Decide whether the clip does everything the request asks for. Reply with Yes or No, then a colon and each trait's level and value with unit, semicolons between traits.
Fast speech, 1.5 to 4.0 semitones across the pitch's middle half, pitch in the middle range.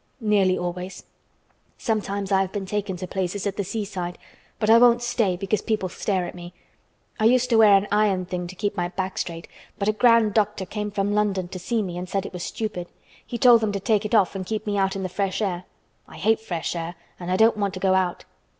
No: fast, 240 wpm; average, 2.7 semitones; high, 195 Hz